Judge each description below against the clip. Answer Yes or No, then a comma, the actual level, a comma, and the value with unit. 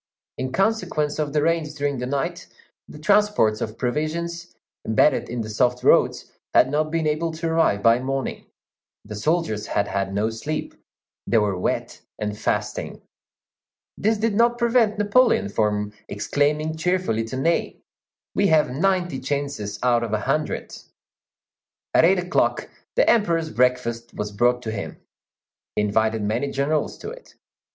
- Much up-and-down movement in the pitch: Yes, wide, 6.9 semitones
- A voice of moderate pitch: Yes, medium, 145 Hz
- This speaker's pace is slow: No, average, 150 wpm